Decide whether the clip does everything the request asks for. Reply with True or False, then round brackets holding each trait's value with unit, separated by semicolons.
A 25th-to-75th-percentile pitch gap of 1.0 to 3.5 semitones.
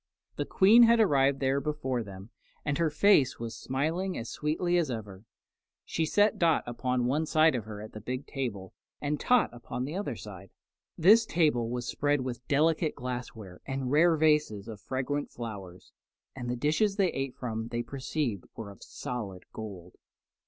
False (5.3 semitones)